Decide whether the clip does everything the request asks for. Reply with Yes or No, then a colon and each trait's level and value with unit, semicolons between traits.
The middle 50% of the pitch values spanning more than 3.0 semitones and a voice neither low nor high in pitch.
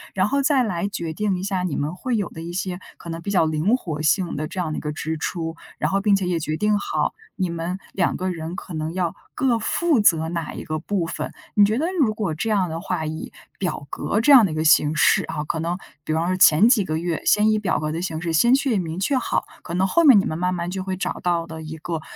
Yes: average, 4.1 semitones; medium, 180 Hz